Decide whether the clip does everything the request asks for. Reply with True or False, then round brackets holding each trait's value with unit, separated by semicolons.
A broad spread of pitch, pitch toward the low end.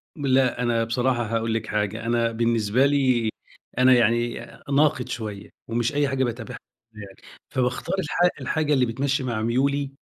False (2.8 semitones; 120 Hz)